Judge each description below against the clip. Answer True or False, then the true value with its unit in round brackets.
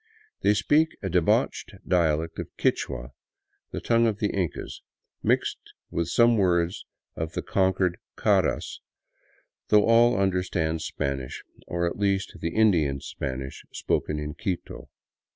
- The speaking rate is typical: False (130 wpm)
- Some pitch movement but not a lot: True (4.4 semitones)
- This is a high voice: False (90 Hz)